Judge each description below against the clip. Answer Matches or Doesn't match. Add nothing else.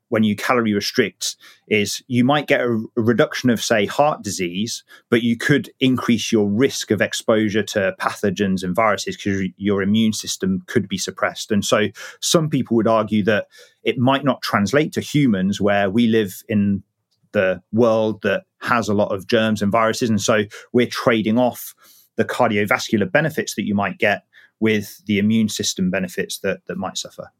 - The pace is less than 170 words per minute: Doesn't match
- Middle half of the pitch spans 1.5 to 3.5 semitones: Matches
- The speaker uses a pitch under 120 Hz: Matches